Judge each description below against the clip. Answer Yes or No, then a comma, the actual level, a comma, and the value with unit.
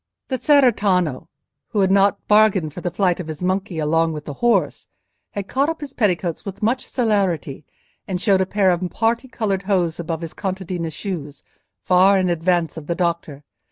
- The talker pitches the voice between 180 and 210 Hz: Yes, medium, 185 Hz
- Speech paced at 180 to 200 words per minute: Yes, average, 185 wpm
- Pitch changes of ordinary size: Yes, average, 3.7 semitones